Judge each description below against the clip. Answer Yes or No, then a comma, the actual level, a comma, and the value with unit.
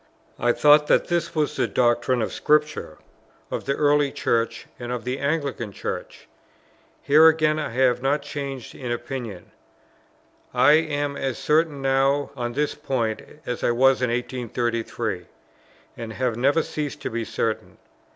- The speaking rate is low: No, average, 150 wpm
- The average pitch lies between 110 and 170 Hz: Yes, low, 135 Hz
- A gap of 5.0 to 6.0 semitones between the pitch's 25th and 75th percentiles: No, average, 3.6 semitones